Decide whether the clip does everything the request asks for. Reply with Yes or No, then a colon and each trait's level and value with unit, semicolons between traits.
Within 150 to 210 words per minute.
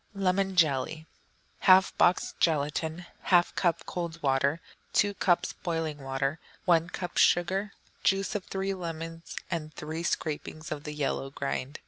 No: slow, 135 wpm